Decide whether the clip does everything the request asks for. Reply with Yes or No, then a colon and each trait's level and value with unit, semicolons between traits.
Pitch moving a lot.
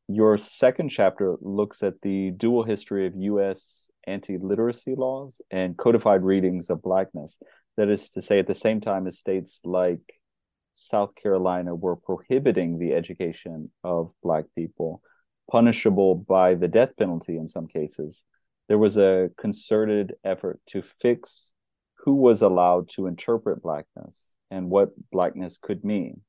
No: average, 2.8 semitones